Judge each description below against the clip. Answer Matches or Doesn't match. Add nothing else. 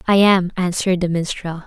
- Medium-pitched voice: Matches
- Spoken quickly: Doesn't match